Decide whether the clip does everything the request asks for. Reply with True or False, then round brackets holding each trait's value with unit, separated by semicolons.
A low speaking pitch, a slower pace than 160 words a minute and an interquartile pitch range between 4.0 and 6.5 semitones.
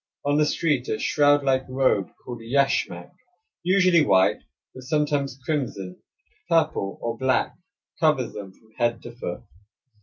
True (130 Hz; 140 wpm; 4.5 semitones)